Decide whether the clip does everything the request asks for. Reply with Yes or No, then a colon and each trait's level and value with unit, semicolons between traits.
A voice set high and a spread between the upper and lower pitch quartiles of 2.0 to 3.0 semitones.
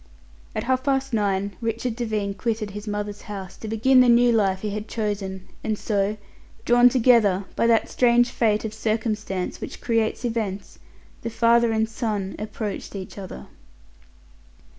Yes: high, 220 Hz; narrow, 2.5 semitones